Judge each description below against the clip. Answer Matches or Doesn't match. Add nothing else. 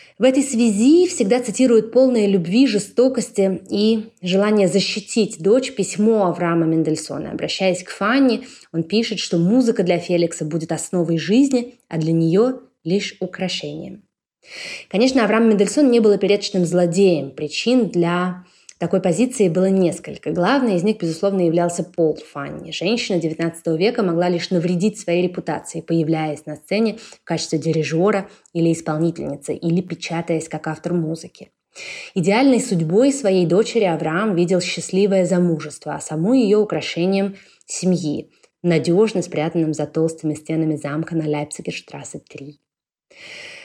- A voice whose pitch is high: Doesn't match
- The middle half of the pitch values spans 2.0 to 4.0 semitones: Doesn't match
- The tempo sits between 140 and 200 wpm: Doesn't match